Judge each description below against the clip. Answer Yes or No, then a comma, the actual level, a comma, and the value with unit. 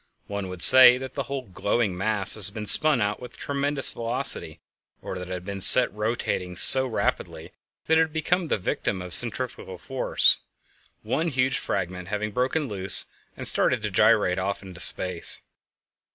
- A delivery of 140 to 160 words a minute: No, average, 170 wpm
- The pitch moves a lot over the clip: Yes, wide, 5.9 semitones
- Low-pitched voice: Yes, low, 105 Hz